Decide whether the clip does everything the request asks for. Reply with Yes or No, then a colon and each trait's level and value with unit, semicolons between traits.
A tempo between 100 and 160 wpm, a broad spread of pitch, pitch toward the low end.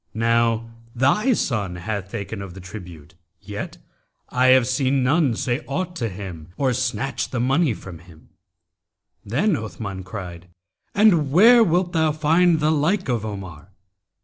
Yes: average, 150 wpm; wide, 7.7 semitones; low, 120 Hz